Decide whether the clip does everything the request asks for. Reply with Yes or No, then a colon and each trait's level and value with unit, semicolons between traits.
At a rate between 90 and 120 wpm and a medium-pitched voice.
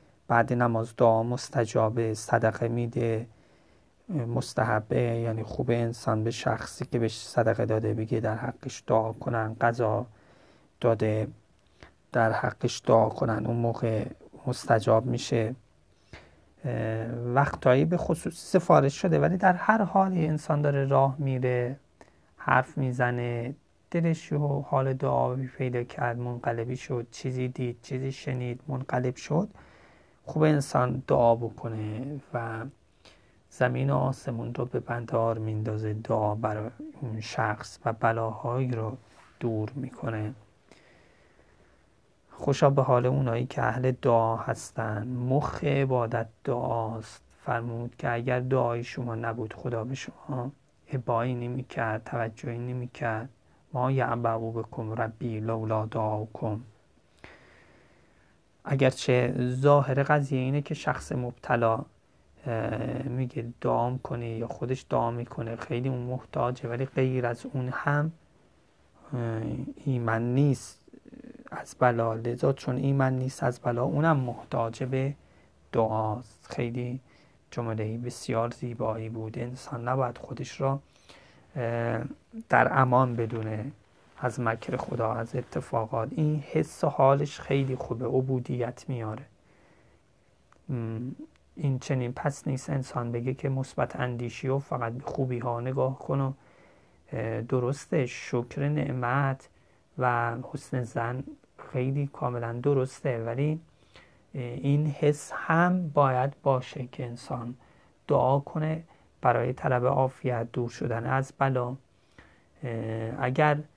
No: average, 115 wpm; low, 125 Hz